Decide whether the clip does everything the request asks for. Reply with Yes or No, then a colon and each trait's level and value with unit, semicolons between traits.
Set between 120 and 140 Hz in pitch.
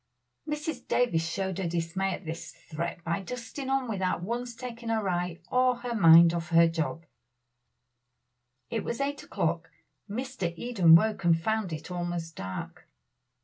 No: high, 190 Hz